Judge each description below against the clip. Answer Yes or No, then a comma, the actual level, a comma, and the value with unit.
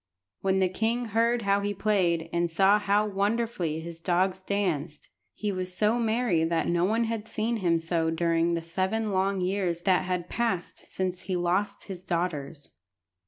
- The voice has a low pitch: No, medium, 185 Hz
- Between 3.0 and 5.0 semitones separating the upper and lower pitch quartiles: Yes, average, 3.4 semitones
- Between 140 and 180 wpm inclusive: Yes, average, 170 wpm